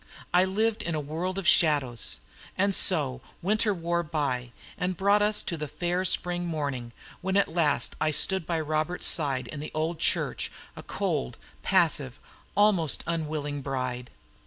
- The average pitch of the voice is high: No, medium, 165 Hz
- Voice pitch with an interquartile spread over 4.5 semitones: No, average, 4.2 semitones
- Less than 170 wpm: Yes, average, 160 wpm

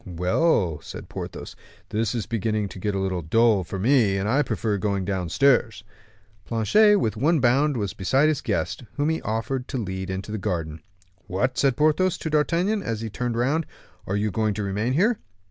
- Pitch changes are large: Yes, wide, 6.0 semitones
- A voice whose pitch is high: No, low, 110 Hz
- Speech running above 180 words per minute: Yes, average, 190 wpm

